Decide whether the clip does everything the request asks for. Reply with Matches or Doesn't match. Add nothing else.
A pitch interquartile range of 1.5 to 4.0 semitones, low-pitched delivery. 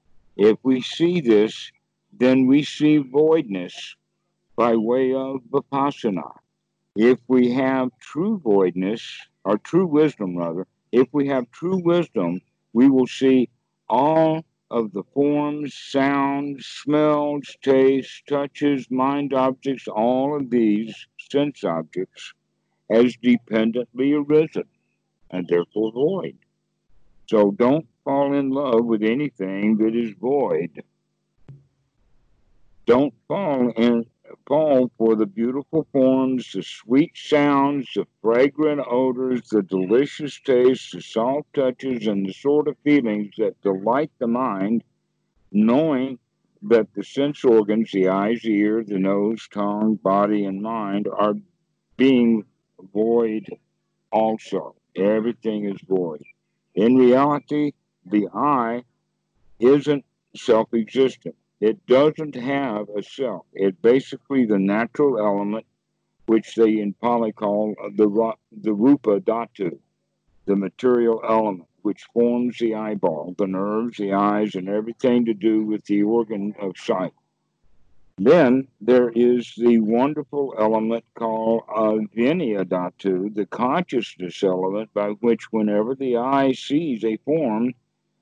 Doesn't match